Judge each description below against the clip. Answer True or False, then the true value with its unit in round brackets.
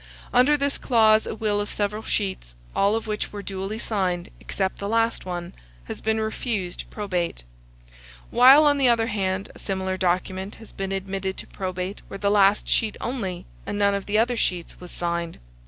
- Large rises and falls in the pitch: False (2.8 semitones)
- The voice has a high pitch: True (200 Hz)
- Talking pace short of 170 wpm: False (185 wpm)